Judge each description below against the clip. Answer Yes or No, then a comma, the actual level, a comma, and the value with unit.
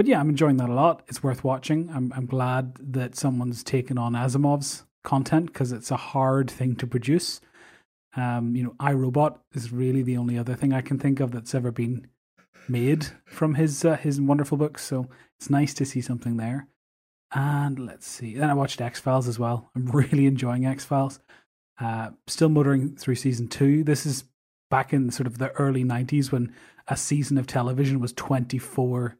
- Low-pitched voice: Yes, low, 130 Hz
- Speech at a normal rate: Yes, average, 195 wpm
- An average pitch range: No, narrow, 2.1 semitones